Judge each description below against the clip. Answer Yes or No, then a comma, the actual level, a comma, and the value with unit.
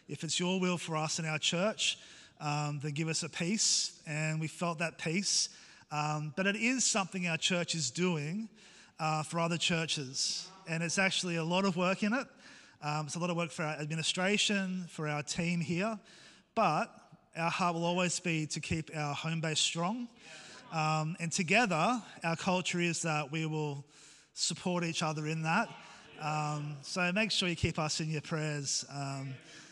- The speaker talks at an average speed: Yes, average, 185 wpm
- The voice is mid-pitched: Yes, medium, 165 Hz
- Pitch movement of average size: Yes, average, 3.0 semitones